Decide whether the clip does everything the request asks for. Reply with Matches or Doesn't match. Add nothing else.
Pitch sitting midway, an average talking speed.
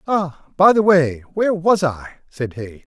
Matches